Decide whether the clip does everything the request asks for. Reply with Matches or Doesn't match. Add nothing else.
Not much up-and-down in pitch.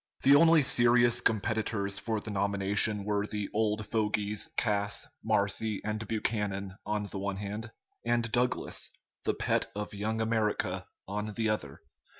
Matches